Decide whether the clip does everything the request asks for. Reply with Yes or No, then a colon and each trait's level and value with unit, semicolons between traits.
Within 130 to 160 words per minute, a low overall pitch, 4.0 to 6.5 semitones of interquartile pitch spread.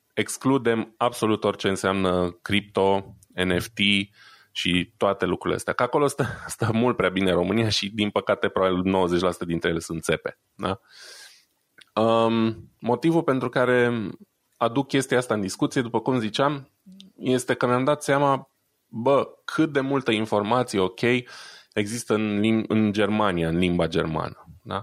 Yes: average, 140 wpm; low, 110 Hz; average, 4.5 semitones